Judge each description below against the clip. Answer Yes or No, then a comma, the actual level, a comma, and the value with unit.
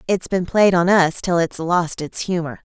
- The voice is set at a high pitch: No, medium, 175 Hz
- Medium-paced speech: No, fast, 220 wpm